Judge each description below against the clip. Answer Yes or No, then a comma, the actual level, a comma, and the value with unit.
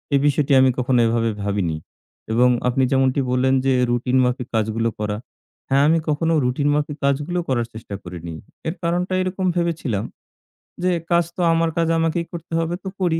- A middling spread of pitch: No, wide, 5.7 semitones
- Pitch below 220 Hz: Yes, low, 135 Hz